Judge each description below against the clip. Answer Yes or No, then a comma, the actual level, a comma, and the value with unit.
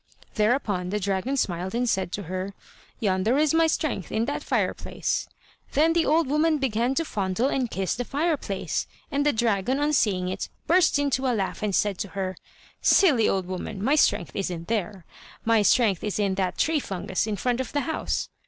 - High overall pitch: Yes, high, 220 Hz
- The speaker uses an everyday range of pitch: No, wide, 6.6 semitones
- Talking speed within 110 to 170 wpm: No, average, 190 wpm